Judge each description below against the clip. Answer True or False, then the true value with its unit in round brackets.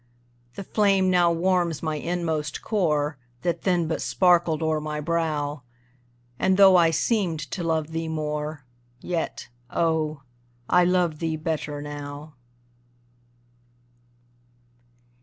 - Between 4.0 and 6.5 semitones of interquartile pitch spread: False (2.7 semitones)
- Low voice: False (160 Hz)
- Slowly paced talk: True (115 wpm)